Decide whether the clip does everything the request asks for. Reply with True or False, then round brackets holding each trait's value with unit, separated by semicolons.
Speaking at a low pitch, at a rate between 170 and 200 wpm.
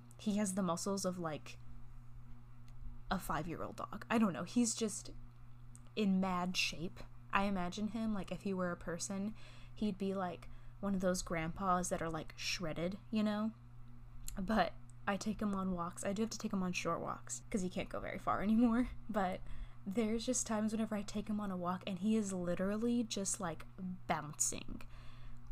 False (180 Hz; 190 wpm)